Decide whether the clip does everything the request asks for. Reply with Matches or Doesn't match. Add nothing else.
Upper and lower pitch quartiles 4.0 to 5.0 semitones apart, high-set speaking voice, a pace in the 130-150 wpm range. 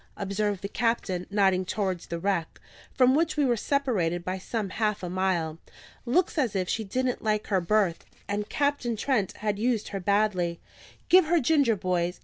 Doesn't match